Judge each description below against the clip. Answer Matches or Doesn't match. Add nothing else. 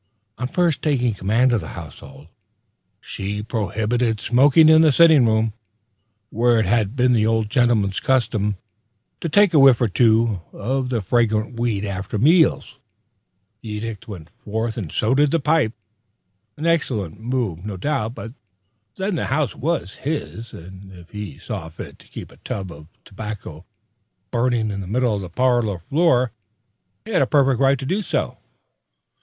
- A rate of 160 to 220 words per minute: Matches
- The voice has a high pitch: Doesn't match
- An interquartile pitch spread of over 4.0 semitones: Matches